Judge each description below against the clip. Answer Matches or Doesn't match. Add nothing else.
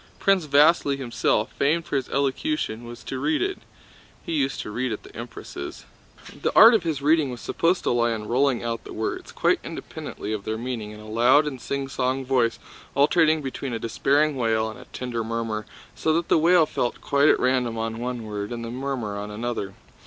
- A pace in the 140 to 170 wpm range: Doesn't match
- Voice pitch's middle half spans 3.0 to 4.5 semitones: Matches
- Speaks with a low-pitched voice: Matches